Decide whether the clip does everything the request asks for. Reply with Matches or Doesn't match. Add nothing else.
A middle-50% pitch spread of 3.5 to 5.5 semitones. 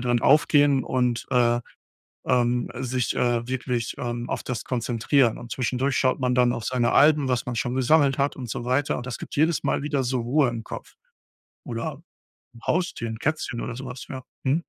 Doesn't match